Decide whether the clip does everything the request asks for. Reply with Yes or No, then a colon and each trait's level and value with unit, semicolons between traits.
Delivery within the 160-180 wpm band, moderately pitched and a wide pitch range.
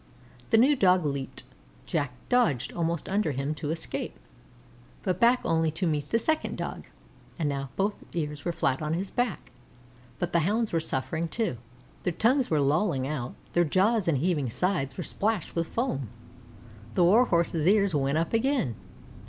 Yes: average, 170 wpm; medium, 170 Hz; wide, 5.9 semitones